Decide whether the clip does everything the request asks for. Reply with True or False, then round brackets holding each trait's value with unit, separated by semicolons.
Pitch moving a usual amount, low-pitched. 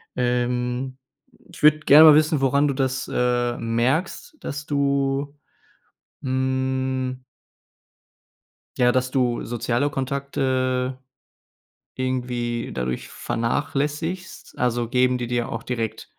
False (2.2 semitones; 130 Hz)